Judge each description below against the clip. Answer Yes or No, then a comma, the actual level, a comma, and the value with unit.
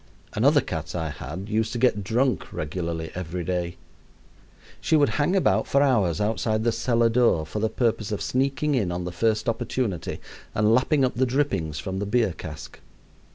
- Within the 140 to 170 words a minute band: No, average, 180 wpm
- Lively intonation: Yes, wide, 6.1 semitones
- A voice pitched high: No, low, 110 Hz